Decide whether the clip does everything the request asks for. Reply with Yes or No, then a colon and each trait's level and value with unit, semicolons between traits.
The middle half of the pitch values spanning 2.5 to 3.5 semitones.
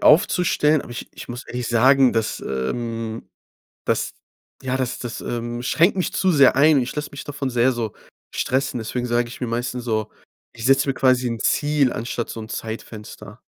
Yes: average, 2.8 semitones